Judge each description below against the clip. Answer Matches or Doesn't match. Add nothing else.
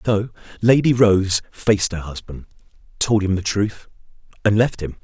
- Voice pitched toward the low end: Matches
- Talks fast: Doesn't match